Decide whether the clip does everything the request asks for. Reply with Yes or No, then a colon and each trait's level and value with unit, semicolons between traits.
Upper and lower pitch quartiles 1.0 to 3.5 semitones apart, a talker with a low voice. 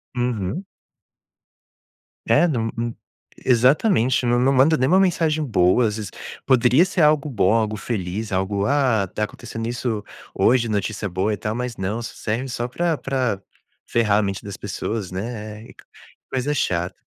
No: average, 3.9 semitones; low, 115 Hz